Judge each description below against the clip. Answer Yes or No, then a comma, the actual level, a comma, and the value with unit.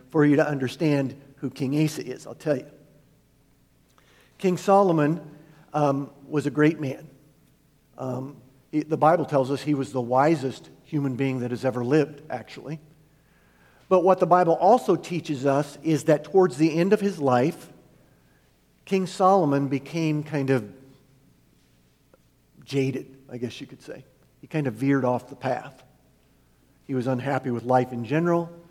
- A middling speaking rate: Yes, average, 155 wpm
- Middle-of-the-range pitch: Yes, medium, 145 Hz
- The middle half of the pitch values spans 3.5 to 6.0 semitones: No, average, 2.9 semitones